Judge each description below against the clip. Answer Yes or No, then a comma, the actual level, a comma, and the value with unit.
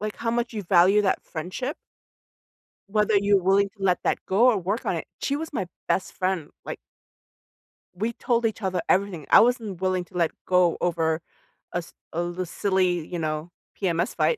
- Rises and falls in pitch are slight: No, average, 3.4 semitones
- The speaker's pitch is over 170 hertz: Yes, high, 190 Hz